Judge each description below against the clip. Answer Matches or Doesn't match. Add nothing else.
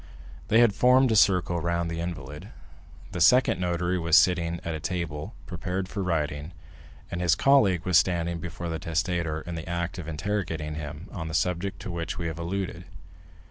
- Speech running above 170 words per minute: Matches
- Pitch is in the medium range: Doesn't match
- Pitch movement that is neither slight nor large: Doesn't match